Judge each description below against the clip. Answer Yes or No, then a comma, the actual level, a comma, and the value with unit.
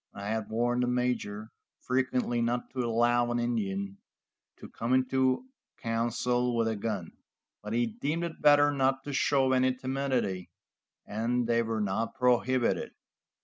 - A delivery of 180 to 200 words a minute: No, average, 145 wpm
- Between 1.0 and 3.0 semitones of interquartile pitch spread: Yes, narrow, 2.4 semitones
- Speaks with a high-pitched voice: No, low, 120 Hz